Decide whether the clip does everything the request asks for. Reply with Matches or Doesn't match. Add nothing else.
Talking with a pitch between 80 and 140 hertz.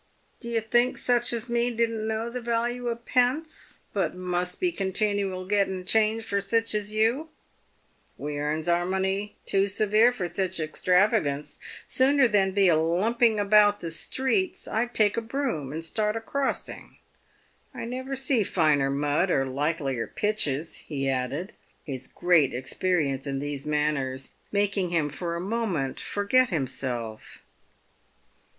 Doesn't match